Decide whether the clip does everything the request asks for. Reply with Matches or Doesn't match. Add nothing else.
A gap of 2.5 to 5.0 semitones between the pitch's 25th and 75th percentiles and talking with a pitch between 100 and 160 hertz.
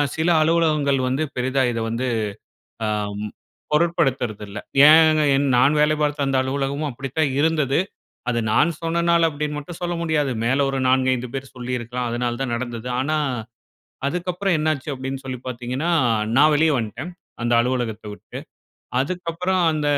Matches